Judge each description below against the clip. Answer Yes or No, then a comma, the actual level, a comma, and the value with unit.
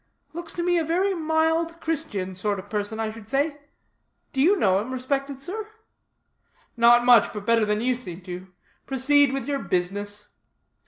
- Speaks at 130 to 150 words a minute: No, average, 165 wpm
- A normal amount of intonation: No, wide, 7.4 semitones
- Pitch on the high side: Yes, very high, 255 Hz